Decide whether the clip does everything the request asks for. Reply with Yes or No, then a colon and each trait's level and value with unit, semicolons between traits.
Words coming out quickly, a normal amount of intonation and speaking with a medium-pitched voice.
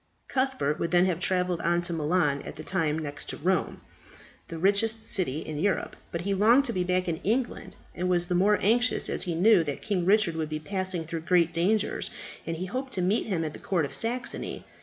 Yes: fast, 225 wpm; average, 3.8 semitones; medium, 180 Hz